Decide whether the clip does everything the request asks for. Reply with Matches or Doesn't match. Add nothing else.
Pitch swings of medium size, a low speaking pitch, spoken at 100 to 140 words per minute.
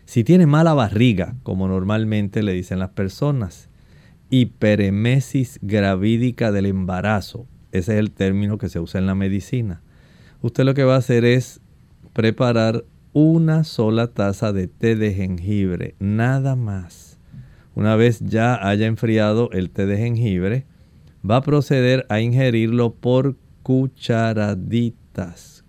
Matches